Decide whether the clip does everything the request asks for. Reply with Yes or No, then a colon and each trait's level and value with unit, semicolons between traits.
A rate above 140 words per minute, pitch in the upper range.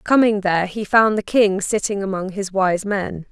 Yes: average, 200 wpm; high, 200 Hz